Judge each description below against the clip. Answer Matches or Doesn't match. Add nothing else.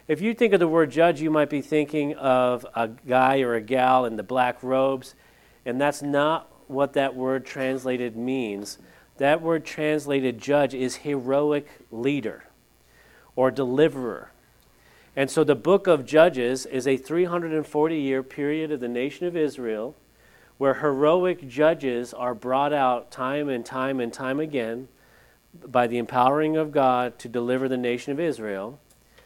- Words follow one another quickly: Doesn't match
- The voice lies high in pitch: Doesn't match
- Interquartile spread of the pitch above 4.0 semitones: Doesn't match